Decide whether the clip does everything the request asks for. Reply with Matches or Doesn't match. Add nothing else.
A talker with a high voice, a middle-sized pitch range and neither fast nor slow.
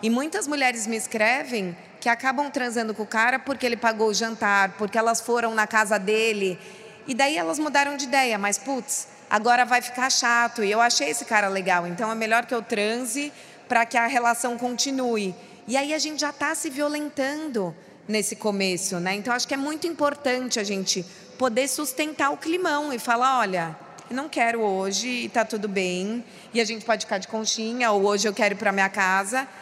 Doesn't match